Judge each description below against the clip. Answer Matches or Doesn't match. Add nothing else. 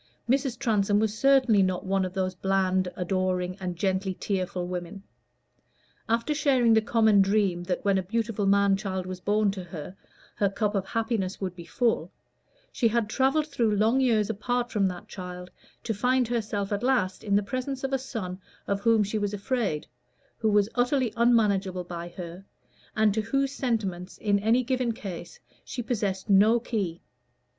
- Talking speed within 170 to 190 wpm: Matches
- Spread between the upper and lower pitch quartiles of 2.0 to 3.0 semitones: Doesn't match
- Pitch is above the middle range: Matches